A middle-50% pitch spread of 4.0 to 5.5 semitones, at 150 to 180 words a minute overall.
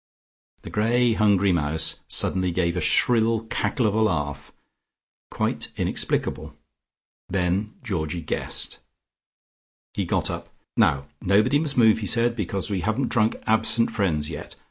No: average, 4.8 semitones; slow, 135 wpm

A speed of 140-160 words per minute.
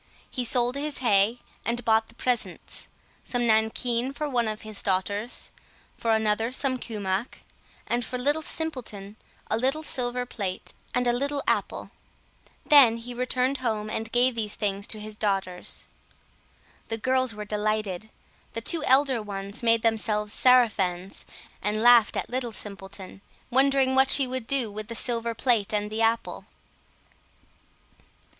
Yes: average, 150 wpm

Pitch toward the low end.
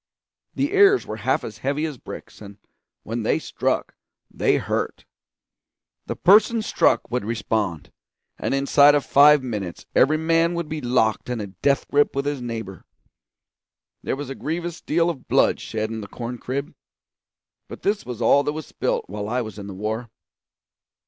Yes: low, 130 Hz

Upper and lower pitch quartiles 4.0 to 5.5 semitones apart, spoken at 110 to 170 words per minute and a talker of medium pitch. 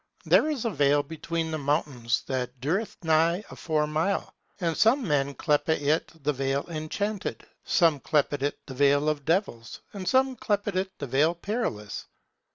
Yes: average, 4.8 semitones; average, 165 wpm; medium, 155 Hz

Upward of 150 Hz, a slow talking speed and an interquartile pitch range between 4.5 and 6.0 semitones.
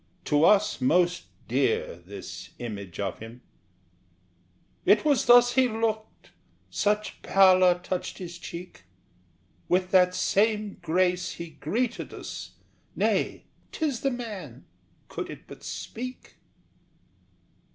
Yes: medium, 185 Hz; slow, 110 wpm; average, 4.9 semitones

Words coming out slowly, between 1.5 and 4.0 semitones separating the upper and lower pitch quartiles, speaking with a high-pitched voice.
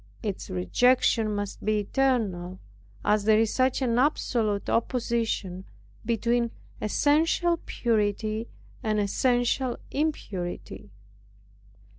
Yes: slow, 90 wpm; average, 3.5 semitones; high, 225 Hz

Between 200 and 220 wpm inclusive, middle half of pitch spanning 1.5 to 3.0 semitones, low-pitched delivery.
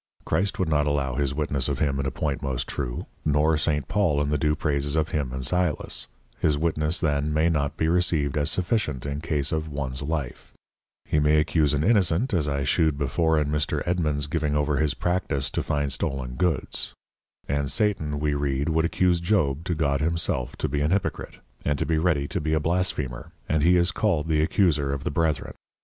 Yes: fast, 205 wpm; narrow, 2.5 semitones; very low, 75 Hz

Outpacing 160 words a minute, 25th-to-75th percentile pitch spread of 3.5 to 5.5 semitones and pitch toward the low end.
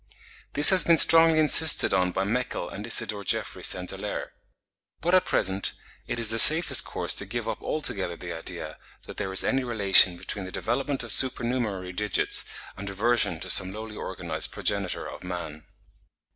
Yes: average, 170 wpm; average, 5.1 semitones; low, 105 Hz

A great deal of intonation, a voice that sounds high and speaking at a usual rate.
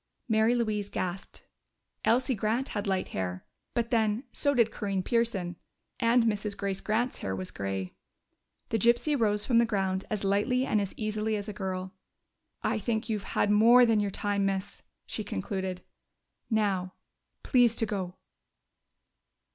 No: average, 3.2 semitones; high, 210 Hz; average, 155 wpm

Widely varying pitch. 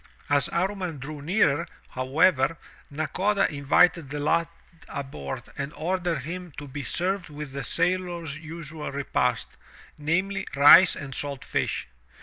No: average, 4.1 semitones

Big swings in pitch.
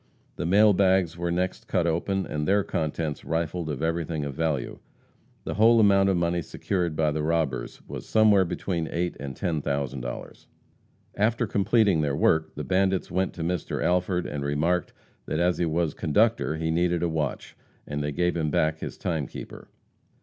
No: average, 3.2 semitones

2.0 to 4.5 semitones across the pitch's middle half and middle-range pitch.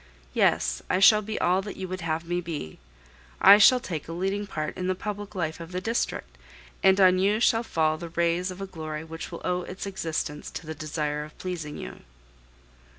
Yes: average, 3.5 semitones; medium, 180 Hz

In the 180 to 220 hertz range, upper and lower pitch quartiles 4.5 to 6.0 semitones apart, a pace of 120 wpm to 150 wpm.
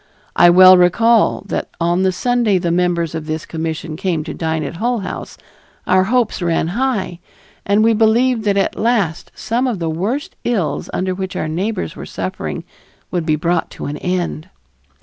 No: medium, 185 Hz; average, 4.8 semitones; average, 180 wpm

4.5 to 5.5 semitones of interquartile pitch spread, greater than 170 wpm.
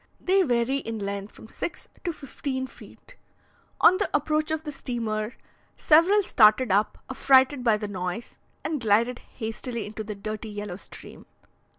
No: average, 5.1 semitones; average, 155 wpm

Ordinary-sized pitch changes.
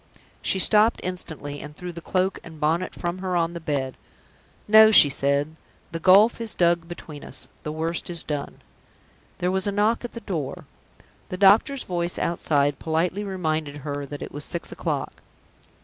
Yes: average, 3.9 semitones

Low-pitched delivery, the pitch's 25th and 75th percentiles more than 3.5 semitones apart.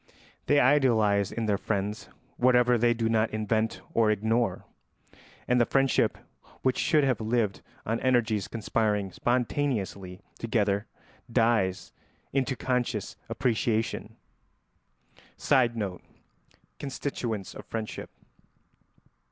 No: low, 115 Hz; average, 2.7 semitones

